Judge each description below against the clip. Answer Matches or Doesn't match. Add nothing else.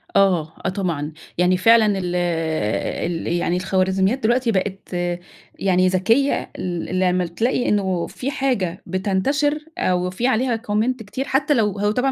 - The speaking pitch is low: Doesn't match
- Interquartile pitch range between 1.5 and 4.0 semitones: Doesn't match